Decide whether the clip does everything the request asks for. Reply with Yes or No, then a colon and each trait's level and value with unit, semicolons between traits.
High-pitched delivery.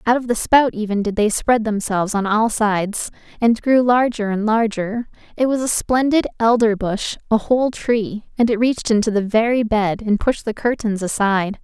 Yes: high, 220 Hz